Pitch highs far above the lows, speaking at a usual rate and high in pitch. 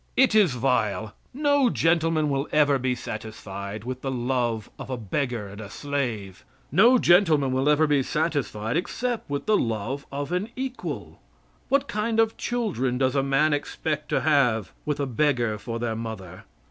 No: wide, 6.1 semitones; average, 170 wpm; low, 135 Hz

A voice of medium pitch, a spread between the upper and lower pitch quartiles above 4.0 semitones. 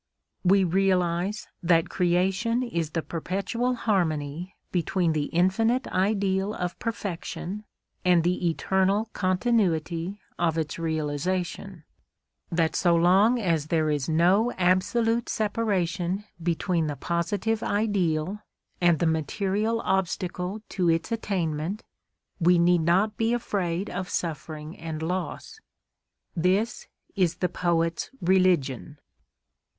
No: medium, 180 Hz; average, 3.3 semitones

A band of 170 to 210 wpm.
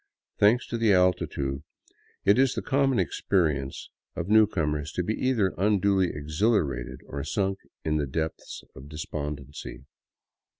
No: average, 140 wpm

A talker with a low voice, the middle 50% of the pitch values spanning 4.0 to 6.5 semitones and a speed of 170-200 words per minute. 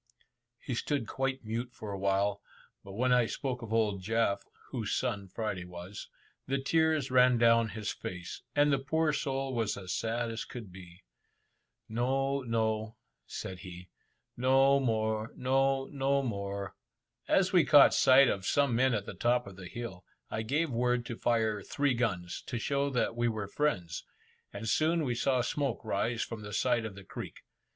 Yes: low, 115 Hz; average, 4.4 semitones; average, 175 wpm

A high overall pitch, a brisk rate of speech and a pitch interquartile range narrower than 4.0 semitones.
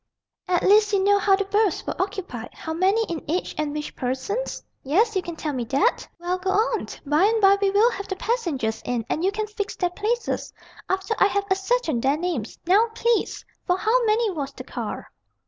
No: very high, 385 Hz; fast, 210 wpm; average, 4.8 semitones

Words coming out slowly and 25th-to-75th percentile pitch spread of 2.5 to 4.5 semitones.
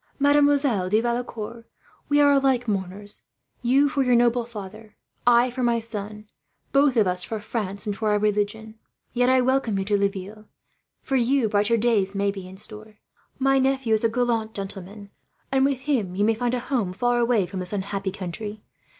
No: average, 185 wpm; average, 3.5 semitones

